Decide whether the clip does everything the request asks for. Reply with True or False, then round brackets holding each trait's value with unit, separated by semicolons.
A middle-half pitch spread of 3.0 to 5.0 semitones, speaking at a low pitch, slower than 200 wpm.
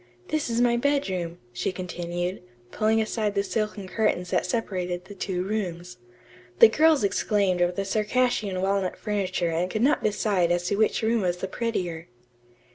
False (3.5 semitones; 195 Hz; 165 wpm)